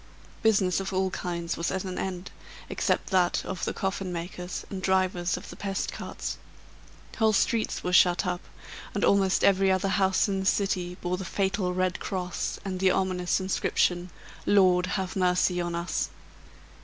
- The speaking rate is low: No, average, 165 wpm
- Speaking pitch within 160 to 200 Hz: Yes, medium, 185 Hz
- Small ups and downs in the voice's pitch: Yes, narrow, 1.3 semitones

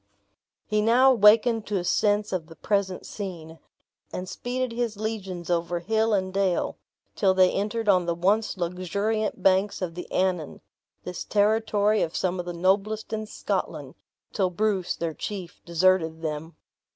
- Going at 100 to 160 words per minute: Yes, average, 155 wpm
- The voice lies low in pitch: No, high, 195 Hz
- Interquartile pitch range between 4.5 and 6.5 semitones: No, average, 3.3 semitones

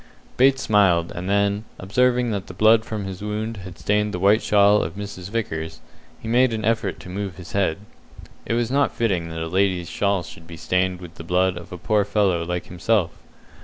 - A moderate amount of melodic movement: Yes, average, 3.3 semitones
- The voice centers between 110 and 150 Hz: No, low, 100 Hz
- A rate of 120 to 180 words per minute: No, fast, 205 wpm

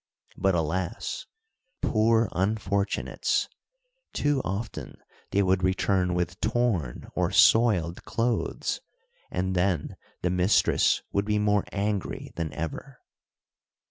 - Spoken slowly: Yes, slow, 105 wpm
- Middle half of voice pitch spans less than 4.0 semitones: Yes, average, 3.2 semitones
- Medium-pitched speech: No, low, 100 Hz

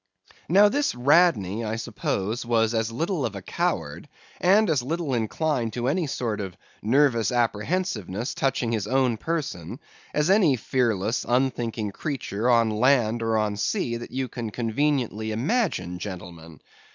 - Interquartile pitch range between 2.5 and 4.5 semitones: No, average, 5.0 semitones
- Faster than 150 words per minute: No, average, 145 wpm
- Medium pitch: No, low, 120 Hz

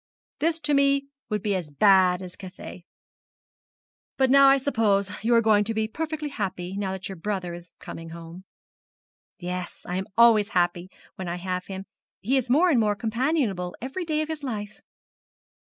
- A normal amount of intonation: No, wide, 6.5 semitones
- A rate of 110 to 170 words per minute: No, average, 180 wpm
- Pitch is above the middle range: Yes, high, 205 Hz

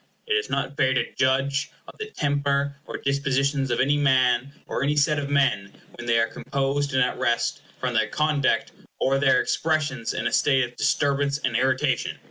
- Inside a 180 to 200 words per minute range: Yes, average, 190 wpm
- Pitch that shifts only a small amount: Yes, narrow, 1.8 semitones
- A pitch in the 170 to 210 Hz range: No, medium, 140 Hz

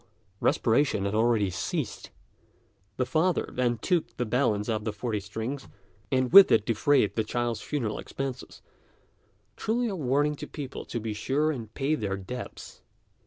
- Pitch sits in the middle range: No, low, 120 Hz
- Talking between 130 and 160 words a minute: Yes, average, 155 wpm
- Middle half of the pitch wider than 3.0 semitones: Yes, average, 4.8 semitones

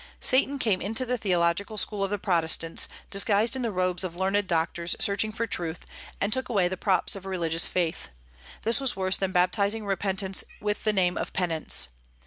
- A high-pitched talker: Yes, high, 195 Hz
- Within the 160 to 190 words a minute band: Yes, average, 185 wpm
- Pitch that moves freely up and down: No, average, 3.2 semitones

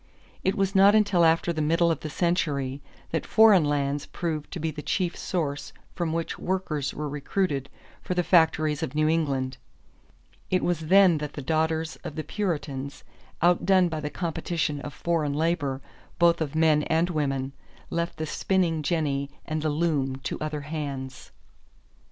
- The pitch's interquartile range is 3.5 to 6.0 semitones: No, average, 2.8 semitones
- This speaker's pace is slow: No, average, 165 wpm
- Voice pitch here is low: No, medium, 160 Hz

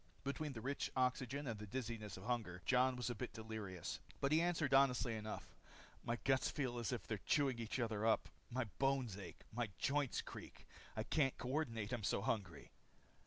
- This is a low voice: Yes, low, 120 Hz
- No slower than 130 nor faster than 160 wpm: No, average, 185 wpm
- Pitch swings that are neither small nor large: Yes, average, 3.6 semitones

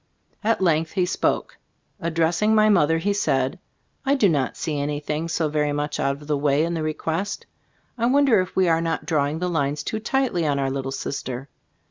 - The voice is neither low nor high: Yes, medium, 160 Hz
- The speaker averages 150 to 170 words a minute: No, average, 195 wpm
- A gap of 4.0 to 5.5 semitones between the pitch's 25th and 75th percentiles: Yes, average, 4.3 semitones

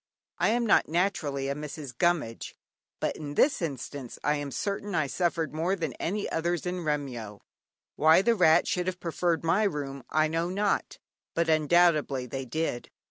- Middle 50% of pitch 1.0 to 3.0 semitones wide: No, average, 3.7 semitones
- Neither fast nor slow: Yes, average, 170 wpm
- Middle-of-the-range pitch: Yes, medium, 160 Hz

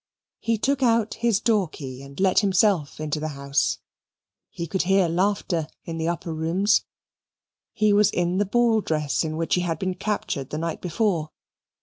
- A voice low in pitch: No, medium, 180 Hz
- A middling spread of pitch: Yes, average, 4.8 semitones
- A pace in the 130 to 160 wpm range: No, average, 180 wpm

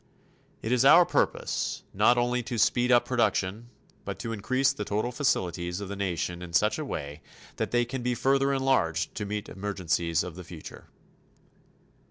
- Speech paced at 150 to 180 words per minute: Yes, average, 175 wpm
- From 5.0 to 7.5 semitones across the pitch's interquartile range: Yes, wide, 5.6 semitones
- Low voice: Yes, low, 110 Hz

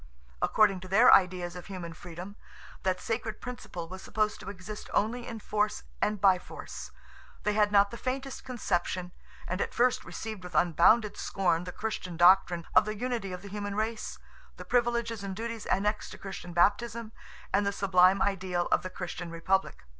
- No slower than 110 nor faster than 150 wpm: No, average, 175 wpm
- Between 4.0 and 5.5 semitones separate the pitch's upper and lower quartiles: No, average, 3.2 semitones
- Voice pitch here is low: No, high, 200 Hz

